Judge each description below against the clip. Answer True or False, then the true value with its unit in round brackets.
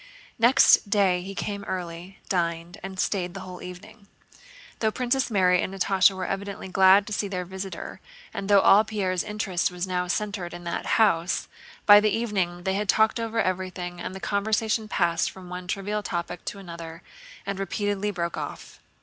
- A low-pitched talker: False (190 Hz)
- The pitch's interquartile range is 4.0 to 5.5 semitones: False (2.4 semitones)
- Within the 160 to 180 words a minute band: True (175 wpm)